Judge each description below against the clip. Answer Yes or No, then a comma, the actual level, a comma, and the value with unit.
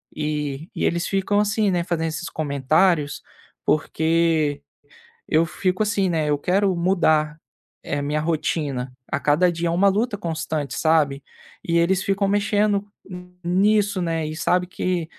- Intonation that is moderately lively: Yes, average, 3.8 semitones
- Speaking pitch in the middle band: Yes, medium, 170 Hz